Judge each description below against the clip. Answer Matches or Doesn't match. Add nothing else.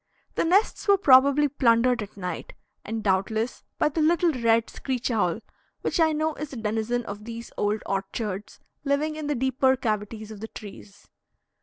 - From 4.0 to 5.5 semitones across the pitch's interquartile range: Matches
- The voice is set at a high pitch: Matches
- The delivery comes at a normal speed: Matches